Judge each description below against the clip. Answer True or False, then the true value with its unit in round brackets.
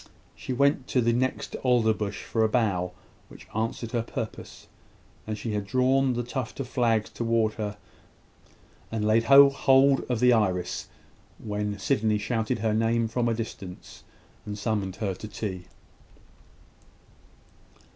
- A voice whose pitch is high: False (115 Hz)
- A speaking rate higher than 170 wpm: False (145 wpm)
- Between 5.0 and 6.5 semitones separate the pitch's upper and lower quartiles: False (2.8 semitones)